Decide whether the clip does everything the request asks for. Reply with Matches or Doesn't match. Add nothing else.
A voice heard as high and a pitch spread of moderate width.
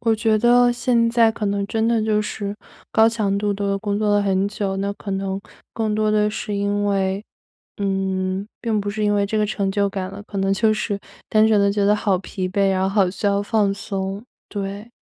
Doesn't match